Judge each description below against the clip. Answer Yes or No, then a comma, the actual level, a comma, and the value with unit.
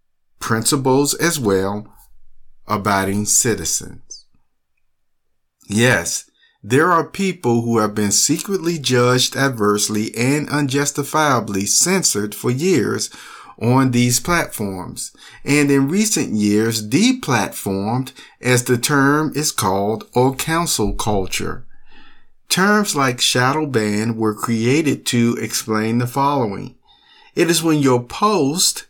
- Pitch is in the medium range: No, low, 125 Hz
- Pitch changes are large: Yes, wide, 5.8 semitones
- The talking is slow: Yes, slow, 105 wpm